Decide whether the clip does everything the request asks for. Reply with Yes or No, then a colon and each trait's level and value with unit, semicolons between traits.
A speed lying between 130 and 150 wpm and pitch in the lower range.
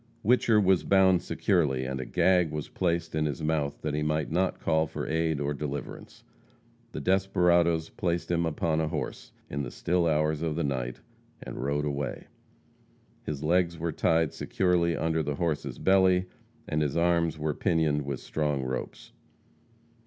No: average, 165 wpm; very low, 80 Hz